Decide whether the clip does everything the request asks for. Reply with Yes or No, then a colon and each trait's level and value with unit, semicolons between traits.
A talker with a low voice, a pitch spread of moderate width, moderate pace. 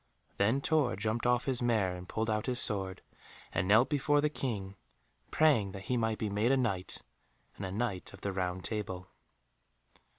Yes: low, 110 Hz; average, 4.3 semitones; average, 185 wpm